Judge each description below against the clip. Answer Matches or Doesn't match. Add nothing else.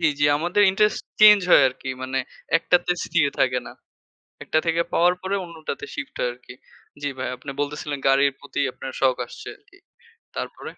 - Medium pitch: Matches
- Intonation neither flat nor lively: Doesn't match